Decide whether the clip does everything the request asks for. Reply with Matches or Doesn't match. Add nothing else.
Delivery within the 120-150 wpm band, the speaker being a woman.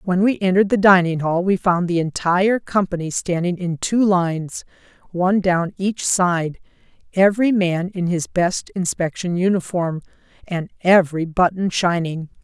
Matches